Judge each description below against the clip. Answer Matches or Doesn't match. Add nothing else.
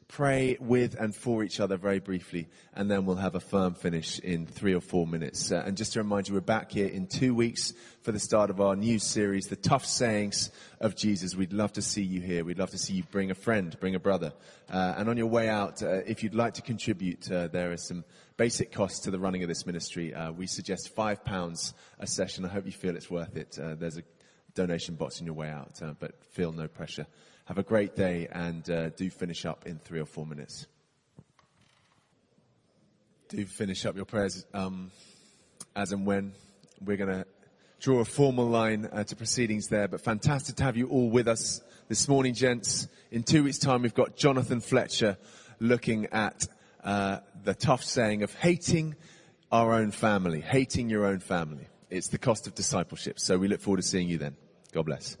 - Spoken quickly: Matches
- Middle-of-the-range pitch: Doesn't match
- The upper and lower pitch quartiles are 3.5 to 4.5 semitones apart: Matches